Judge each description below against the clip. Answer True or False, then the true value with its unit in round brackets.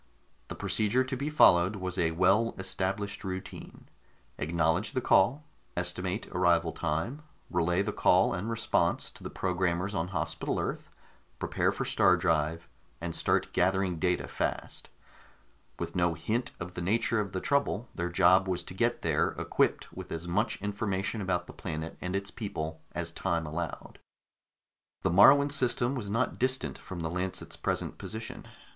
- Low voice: True (95 Hz)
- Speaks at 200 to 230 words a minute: False (160 wpm)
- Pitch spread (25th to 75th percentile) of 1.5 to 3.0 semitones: False (3.8 semitones)